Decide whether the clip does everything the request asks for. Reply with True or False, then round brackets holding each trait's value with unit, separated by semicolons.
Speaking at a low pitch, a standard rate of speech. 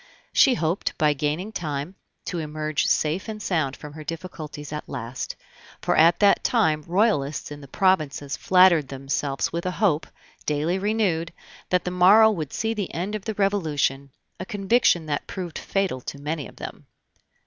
False (165 Hz; 170 wpm)